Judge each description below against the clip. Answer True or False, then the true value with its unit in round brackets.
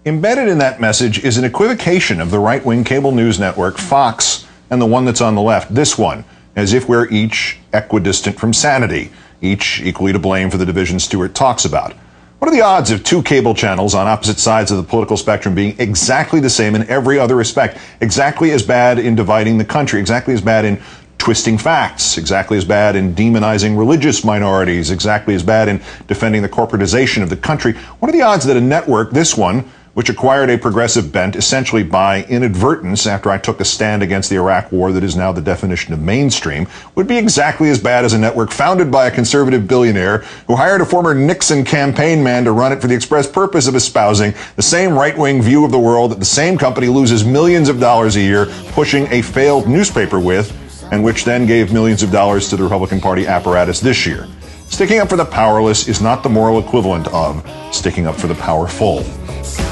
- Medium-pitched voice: False (110 Hz)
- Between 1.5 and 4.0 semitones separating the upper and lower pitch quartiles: False (4.7 semitones)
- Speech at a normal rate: False (210 wpm)